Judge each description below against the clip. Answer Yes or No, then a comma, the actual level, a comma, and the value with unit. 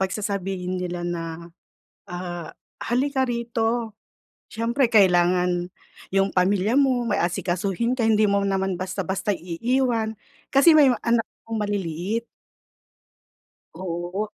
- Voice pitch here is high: Yes, high, 200 Hz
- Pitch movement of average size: Yes, average, 4.4 semitones